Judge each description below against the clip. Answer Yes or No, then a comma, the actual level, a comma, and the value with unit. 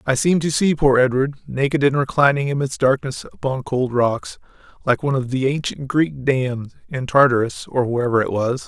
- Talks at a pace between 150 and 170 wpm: No, average, 185 wpm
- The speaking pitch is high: No, low, 135 Hz